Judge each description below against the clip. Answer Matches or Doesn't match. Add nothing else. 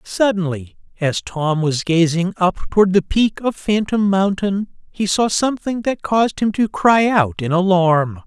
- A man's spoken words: Matches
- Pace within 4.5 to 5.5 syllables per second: Doesn't match